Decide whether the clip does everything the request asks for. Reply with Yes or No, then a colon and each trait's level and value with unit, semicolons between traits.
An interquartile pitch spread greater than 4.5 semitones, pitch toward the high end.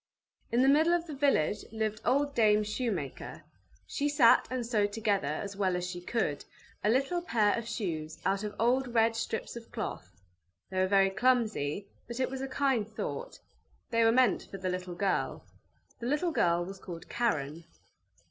Yes: average, 5.2 semitones; high, 220 Hz